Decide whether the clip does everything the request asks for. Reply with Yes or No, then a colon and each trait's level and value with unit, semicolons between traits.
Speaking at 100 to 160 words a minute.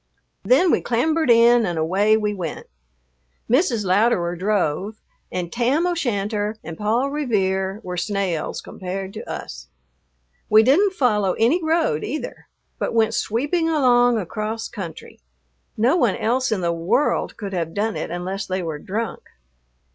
Yes: average, 145 wpm